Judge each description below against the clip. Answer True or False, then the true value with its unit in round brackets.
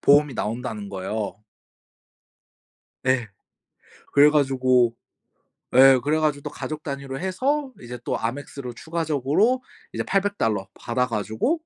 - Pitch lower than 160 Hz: True (135 Hz)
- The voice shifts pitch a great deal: False (4.7 semitones)